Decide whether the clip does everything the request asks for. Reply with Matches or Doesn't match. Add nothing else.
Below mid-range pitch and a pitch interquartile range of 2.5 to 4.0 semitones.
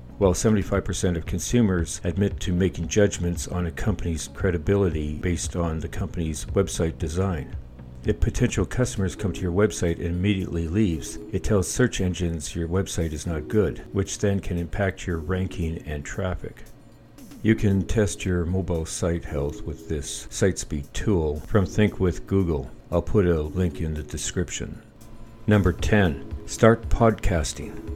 Matches